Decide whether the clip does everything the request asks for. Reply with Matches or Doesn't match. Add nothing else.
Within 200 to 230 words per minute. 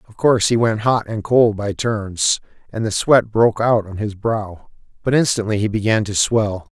Matches